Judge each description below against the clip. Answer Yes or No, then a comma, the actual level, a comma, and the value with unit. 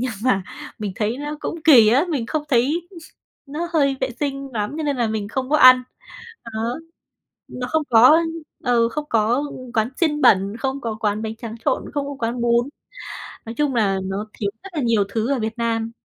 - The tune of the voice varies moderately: Yes, average, 4.2 semitones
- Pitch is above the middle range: Yes, high, 240 Hz